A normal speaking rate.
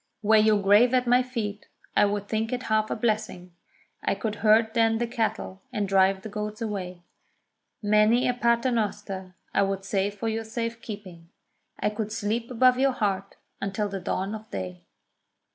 Yes: average, 175 wpm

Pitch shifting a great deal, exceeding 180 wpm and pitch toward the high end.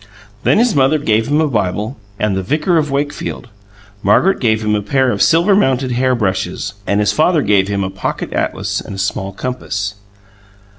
No: wide, 6.1 semitones; average, 190 wpm; low, 120 Hz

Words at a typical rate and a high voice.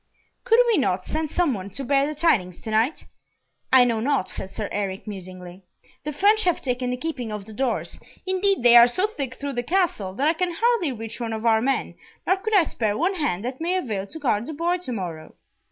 No: fast, 230 wpm; very high, 255 Hz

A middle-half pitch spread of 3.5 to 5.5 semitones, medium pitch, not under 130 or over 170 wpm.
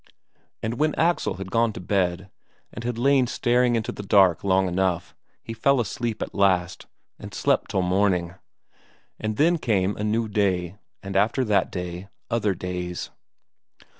No: average, 4.1 semitones; low, 100 Hz; average, 160 wpm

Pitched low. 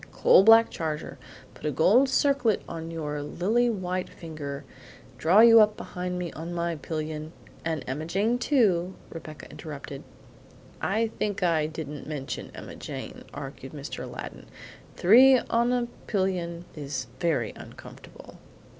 No: medium, 170 Hz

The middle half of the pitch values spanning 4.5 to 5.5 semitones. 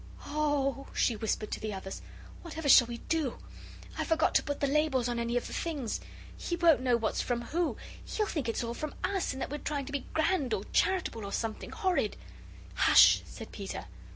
Yes: average, 5.2 semitones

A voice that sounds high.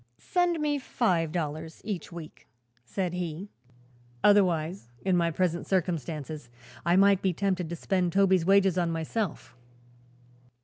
No: medium, 180 Hz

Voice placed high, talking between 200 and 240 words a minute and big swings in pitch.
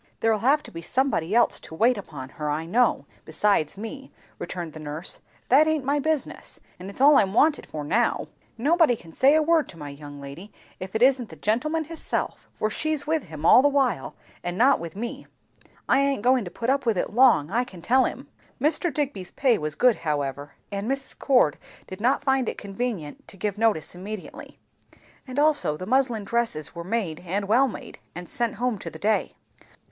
Yes: high, 225 Hz; fast, 205 wpm; wide, 7.4 semitones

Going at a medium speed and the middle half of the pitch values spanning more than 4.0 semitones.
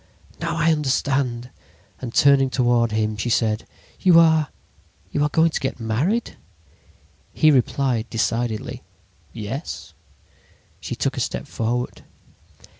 No: slow, 115 wpm; average, 4.6 semitones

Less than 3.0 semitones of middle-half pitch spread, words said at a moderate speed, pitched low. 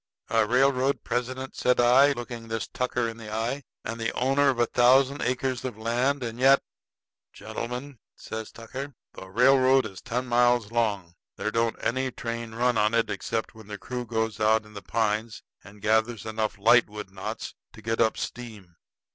Yes: narrow, 2.4 semitones; average, 180 wpm; low, 115 Hz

